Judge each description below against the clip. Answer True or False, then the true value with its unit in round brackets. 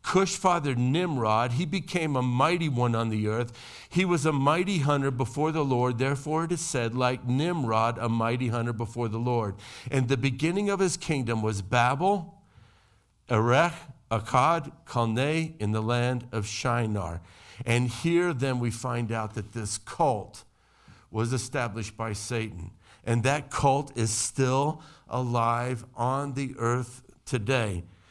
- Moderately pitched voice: False (125 Hz)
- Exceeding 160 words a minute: False (150 wpm)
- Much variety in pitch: False (4.2 semitones)